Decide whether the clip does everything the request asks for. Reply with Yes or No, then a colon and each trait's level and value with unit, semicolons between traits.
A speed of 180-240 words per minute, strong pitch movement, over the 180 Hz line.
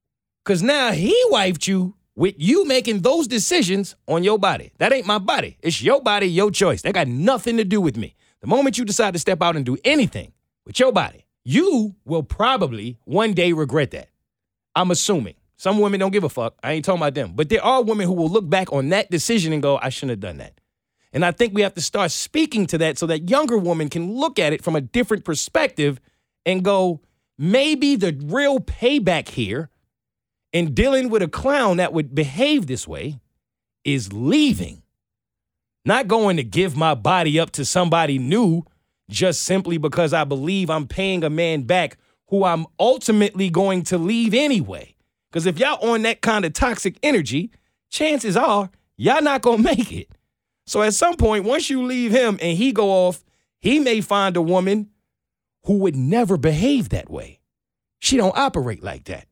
Yes: average, 195 wpm; wide, 6.2 semitones; high, 190 Hz